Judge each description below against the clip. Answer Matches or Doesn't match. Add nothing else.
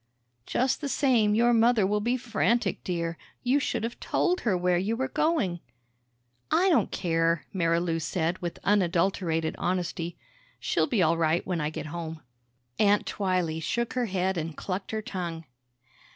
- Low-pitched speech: Doesn't match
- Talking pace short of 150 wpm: Doesn't match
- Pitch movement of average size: Doesn't match